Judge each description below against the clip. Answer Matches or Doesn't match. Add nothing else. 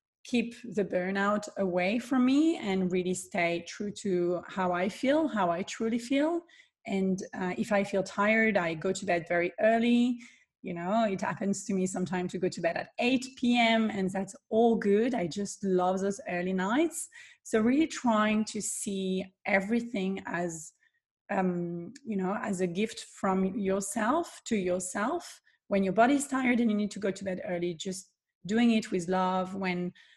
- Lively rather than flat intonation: Doesn't match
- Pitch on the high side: Matches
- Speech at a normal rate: Matches